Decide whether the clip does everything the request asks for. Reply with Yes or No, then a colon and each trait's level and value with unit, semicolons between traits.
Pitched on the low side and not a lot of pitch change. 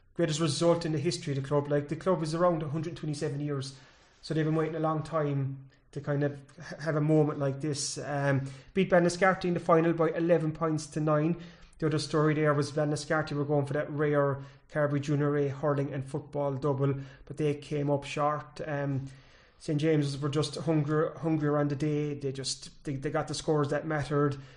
No: medium, 150 Hz; narrow, 1.8 semitones